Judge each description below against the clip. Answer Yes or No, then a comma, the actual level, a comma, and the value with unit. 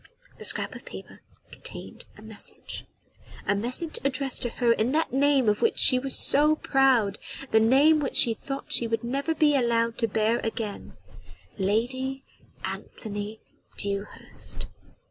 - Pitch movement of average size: Yes, average, 3.7 semitones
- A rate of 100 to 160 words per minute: Yes, average, 145 wpm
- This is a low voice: No, high, 245 Hz